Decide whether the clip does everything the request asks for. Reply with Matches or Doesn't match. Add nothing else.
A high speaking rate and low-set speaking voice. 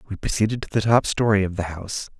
Matches